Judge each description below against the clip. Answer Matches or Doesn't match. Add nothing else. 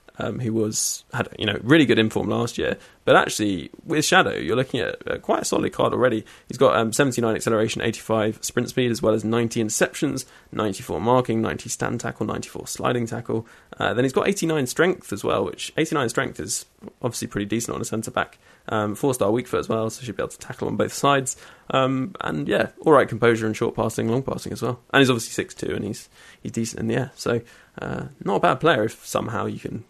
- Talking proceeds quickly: Matches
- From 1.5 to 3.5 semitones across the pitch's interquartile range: Matches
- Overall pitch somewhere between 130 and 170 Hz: Doesn't match